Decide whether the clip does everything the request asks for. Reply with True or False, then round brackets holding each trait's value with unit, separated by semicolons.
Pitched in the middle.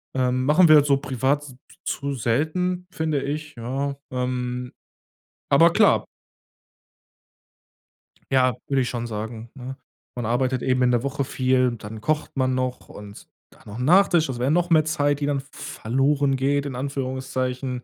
False (130 Hz)